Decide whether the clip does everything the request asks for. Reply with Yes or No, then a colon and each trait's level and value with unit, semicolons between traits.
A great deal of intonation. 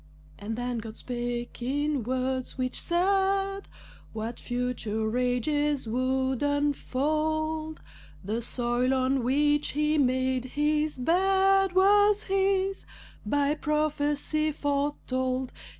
No: average, 3.8 semitones